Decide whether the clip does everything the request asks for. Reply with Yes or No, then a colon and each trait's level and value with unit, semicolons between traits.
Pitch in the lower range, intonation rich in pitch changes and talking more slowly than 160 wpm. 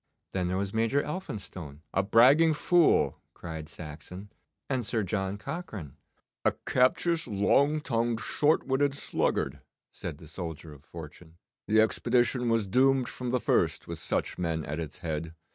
Yes: low, 105 Hz; wide, 7.6 semitones; average, 150 wpm